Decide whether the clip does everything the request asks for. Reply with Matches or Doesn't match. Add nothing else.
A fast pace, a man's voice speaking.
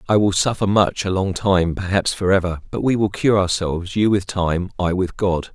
Matches